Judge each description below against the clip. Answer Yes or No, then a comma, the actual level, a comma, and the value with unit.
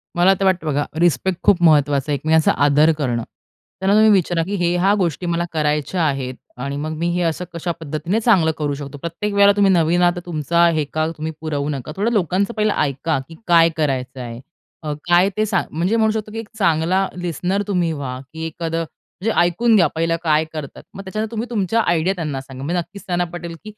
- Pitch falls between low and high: Yes, medium, 170 Hz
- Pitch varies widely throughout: No, average, 3.9 semitones